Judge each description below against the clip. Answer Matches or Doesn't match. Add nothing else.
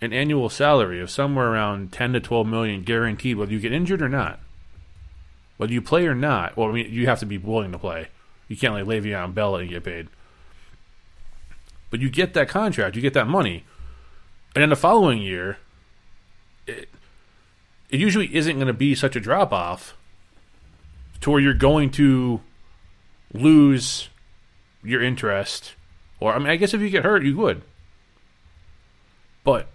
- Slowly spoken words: Doesn't match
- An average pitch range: Doesn't match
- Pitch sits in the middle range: Doesn't match